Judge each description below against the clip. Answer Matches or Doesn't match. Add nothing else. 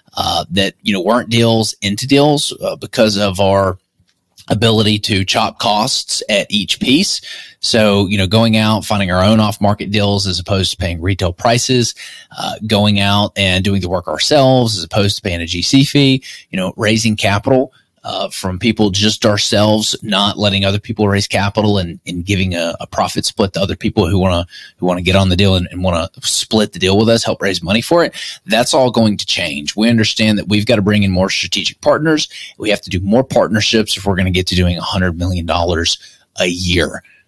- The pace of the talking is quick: Matches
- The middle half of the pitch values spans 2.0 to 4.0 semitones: Matches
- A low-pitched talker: Matches